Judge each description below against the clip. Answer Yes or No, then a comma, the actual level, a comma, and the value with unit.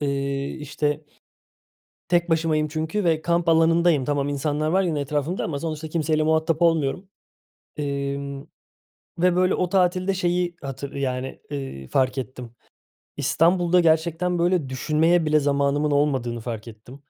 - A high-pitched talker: No, medium, 155 Hz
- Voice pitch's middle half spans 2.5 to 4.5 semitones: Yes, average, 3.4 semitones